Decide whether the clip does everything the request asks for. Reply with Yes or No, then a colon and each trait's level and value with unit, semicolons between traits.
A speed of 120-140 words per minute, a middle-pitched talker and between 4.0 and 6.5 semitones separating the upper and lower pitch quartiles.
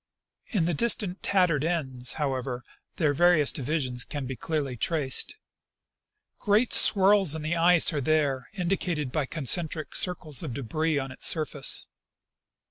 Yes: slow, 135 wpm; medium, 155 Hz; average, 4.4 semitones